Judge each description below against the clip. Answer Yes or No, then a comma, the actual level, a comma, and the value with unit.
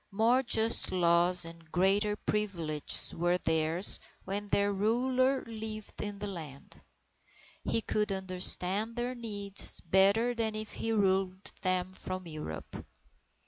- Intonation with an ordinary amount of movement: Yes, average, 3.4 semitones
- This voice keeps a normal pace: No, slow, 125 wpm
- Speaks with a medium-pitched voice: No, high, 200 Hz